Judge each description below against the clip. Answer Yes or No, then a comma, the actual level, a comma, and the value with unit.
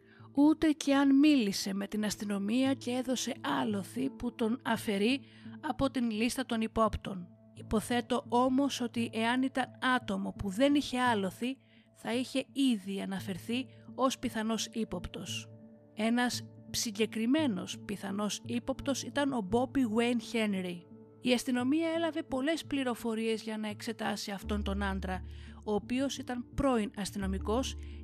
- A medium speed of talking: Yes, average, 130 wpm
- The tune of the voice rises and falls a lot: No, average, 4.4 semitones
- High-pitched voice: Yes, high, 230 Hz